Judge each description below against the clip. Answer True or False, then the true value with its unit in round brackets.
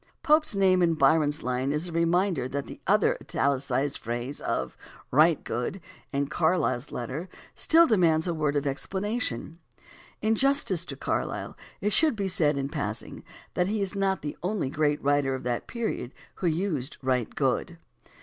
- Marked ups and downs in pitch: True (5.7 semitones)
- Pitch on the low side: False (160 Hz)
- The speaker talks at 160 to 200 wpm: True (165 wpm)